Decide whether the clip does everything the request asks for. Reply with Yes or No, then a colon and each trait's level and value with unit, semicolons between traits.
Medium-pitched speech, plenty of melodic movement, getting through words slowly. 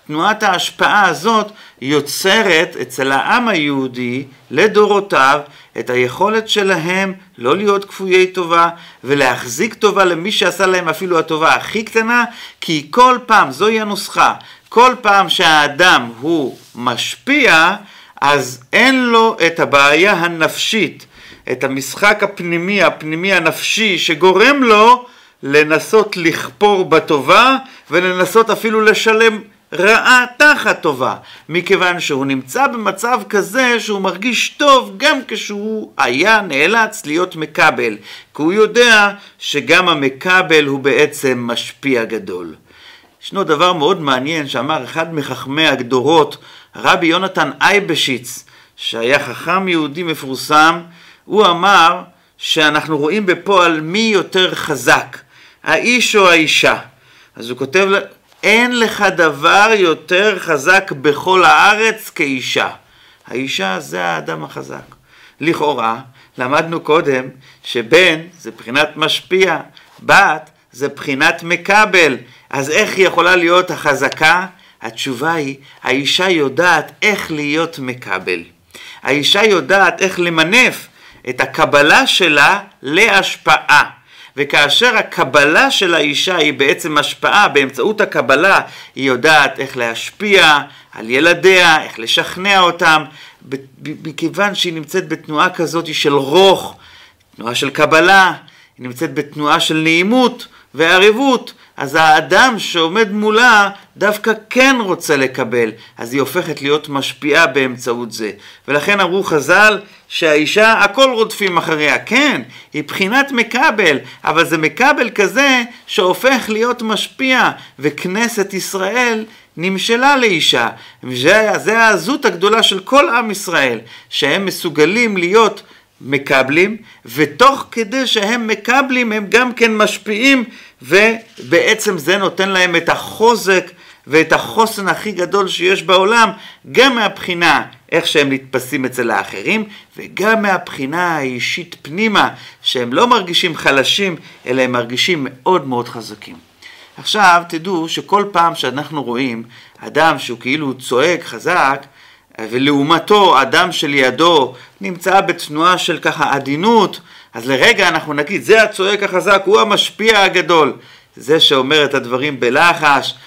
No: medium, 180 Hz; wide, 6.0 semitones; average, 115 wpm